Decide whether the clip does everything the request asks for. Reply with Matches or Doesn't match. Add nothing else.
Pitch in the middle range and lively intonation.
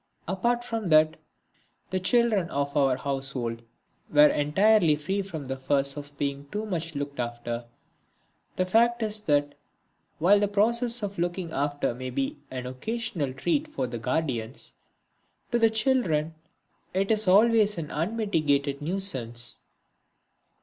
Matches